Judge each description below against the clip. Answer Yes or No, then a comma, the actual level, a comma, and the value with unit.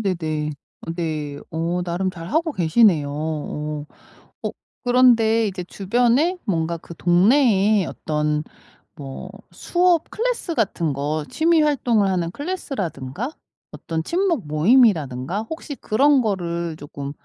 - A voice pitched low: No, medium, 185 Hz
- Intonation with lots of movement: Yes, wide, 7.9 semitones